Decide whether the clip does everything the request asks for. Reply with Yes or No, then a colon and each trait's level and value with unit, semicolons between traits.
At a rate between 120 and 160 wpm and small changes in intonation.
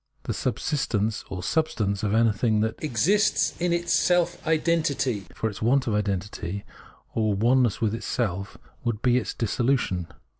No: average, 150 wpm; average, 5.2 semitones